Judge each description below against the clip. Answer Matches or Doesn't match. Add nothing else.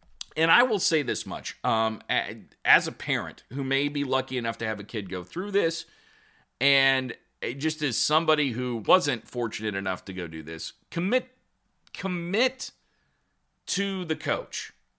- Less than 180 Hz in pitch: Matches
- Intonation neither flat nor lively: Doesn't match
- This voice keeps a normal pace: Matches